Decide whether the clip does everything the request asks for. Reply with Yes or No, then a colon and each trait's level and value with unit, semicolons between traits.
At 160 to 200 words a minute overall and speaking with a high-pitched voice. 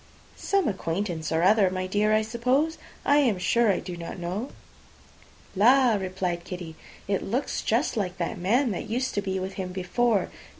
Yes: average, 175 wpm; high, 200 Hz